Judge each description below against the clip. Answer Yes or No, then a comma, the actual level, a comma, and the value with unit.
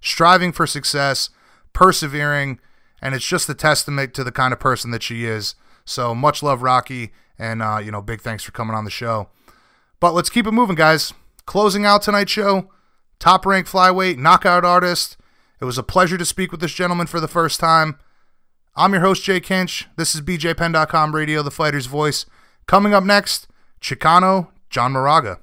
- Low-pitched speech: No, medium, 160 Hz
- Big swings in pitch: Yes, wide, 5.8 semitones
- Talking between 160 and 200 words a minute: Yes, average, 180 wpm